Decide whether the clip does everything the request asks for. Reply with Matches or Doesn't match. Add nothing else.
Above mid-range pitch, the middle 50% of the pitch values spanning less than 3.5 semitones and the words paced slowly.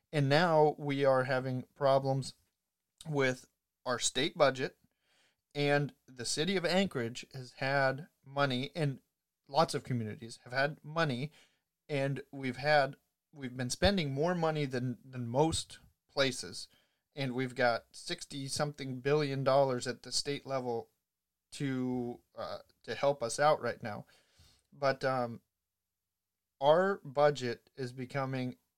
Doesn't match